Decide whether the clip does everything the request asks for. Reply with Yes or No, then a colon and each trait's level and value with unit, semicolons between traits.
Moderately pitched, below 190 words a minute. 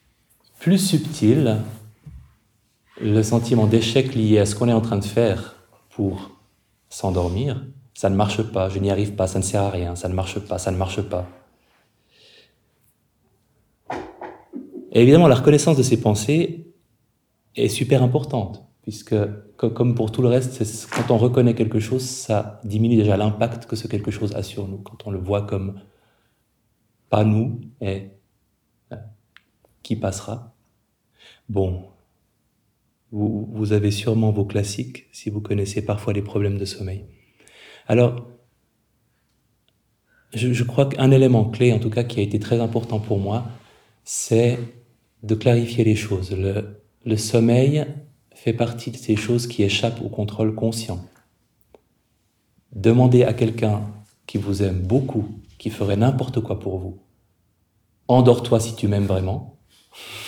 No: low, 110 Hz; slow, 145 wpm